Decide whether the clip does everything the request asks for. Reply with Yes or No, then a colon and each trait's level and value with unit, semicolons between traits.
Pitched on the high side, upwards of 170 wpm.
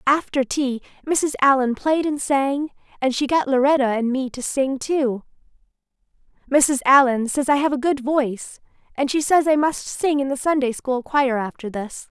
Yes: very high, 270 Hz; average, 180 wpm